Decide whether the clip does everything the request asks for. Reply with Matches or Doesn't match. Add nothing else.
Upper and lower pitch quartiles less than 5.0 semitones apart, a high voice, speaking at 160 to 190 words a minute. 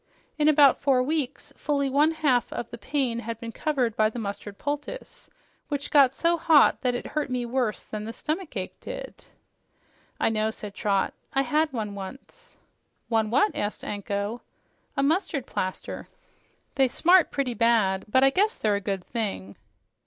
Doesn't match